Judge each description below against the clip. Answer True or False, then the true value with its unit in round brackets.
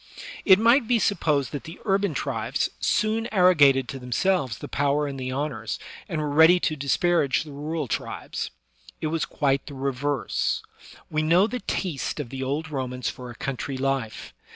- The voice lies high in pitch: False (145 Hz)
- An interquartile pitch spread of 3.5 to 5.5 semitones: True (4.5 semitones)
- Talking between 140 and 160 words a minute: False (175 wpm)